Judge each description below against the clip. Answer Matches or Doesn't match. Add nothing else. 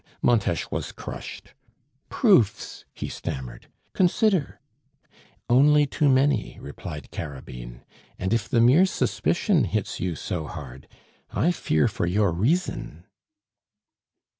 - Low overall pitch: Matches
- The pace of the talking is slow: Matches